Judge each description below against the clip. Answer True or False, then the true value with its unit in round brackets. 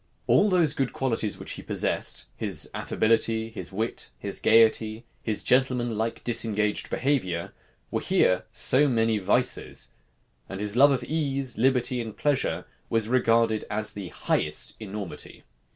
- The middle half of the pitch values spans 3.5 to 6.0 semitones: False (3.1 semitones)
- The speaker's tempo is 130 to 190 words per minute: True (140 wpm)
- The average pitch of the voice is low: True (115 Hz)